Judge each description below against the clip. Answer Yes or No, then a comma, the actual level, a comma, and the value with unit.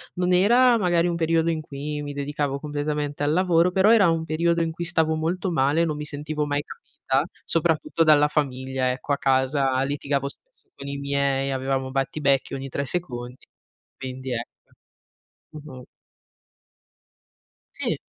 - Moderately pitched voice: Yes, medium, 150 Hz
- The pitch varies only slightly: No, average, 3.4 semitones